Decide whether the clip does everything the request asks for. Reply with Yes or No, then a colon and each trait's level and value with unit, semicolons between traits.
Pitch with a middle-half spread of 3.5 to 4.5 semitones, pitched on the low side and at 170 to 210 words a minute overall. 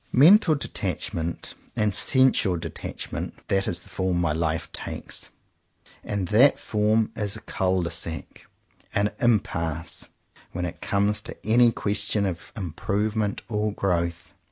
No: average, 4.0 semitones; low, 100 Hz; average, 145 wpm